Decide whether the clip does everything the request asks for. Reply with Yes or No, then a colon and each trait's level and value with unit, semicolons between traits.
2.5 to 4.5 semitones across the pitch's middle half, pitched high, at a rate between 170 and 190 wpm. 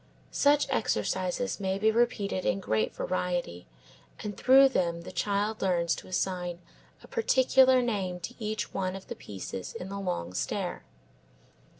No: average, 4.0 semitones; high, 195 Hz; average, 145 wpm